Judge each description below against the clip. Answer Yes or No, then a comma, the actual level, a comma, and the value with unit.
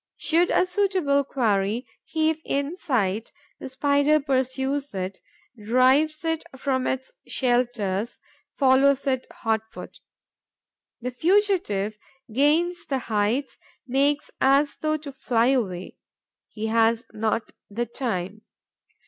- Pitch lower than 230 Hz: No, very high, 260 Hz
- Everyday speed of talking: No, slow, 115 wpm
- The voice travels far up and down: No, average, 4.5 semitones